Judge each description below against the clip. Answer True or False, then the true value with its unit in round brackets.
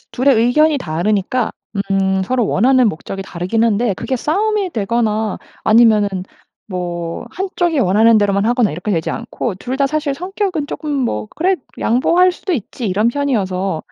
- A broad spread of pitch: True (6.3 semitones)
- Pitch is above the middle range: True (230 Hz)